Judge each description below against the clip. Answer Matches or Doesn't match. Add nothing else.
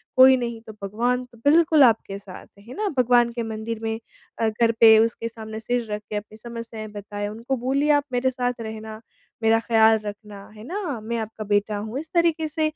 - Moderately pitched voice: Doesn't match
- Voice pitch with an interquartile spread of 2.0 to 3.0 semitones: Matches